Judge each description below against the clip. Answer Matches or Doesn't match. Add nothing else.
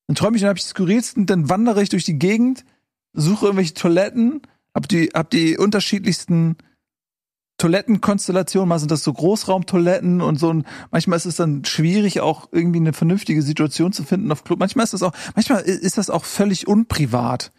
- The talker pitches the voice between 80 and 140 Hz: Doesn't match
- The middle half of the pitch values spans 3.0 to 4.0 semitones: Matches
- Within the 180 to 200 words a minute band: Matches